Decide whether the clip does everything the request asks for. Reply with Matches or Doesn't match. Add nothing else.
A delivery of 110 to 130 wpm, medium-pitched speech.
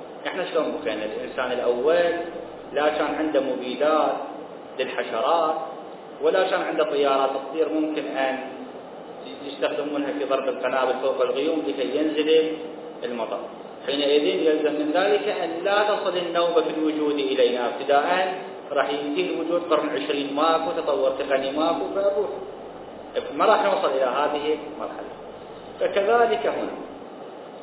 Matches